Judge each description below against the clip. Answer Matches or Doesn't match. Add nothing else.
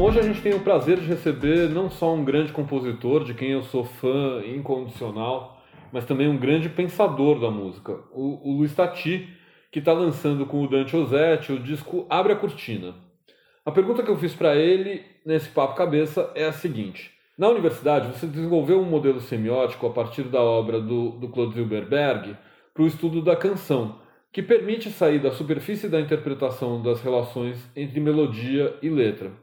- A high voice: Doesn't match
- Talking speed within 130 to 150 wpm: Doesn't match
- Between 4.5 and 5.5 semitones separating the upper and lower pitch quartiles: Matches